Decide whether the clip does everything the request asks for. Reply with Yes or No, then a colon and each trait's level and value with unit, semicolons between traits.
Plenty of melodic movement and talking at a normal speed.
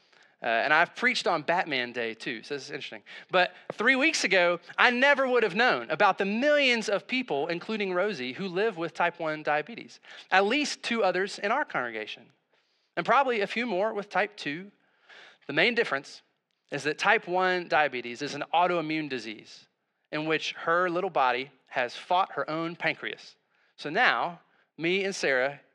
Yes: wide, 6.1 semitones; average, 175 wpm